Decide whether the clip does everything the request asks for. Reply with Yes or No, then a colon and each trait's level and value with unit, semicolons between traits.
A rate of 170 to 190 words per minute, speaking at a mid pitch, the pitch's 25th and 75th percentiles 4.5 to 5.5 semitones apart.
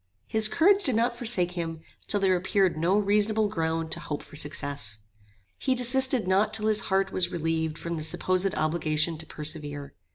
Yes: average, 175 wpm; medium, 180 Hz; average, 5.1 semitones